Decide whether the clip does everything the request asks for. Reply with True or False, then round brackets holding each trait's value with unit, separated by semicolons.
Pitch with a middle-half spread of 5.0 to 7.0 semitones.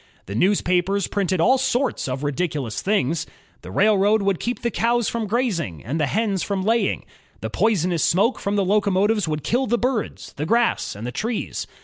True (5.4 semitones)